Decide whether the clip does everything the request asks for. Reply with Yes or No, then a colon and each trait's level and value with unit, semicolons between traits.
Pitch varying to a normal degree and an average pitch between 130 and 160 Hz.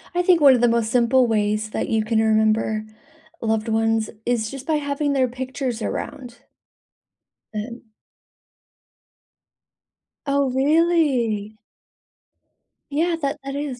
No: average, 4.3 semitones; high, 245 Hz